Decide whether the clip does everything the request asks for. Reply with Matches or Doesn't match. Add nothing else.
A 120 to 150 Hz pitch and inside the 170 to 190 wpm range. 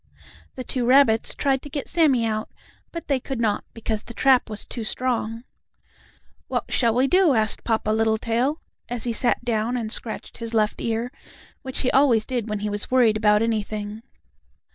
Doesn't match